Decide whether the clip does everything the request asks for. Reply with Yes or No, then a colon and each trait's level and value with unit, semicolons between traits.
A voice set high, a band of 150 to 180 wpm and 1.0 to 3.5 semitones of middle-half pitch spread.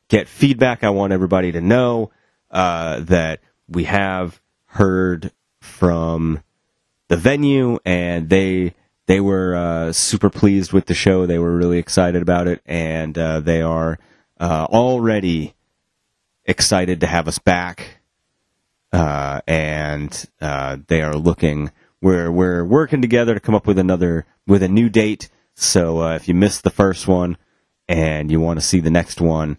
No: very low, 90 Hz; average, 155 wpm; average, 3.2 semitones